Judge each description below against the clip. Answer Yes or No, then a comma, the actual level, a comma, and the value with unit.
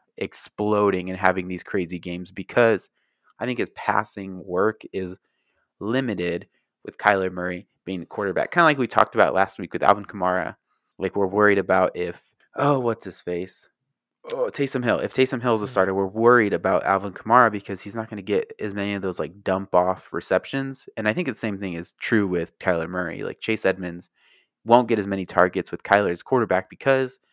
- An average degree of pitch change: Yes, average, 3.5 semitones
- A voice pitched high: No, low, 100 Hz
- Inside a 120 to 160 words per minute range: No, average, 200 wpm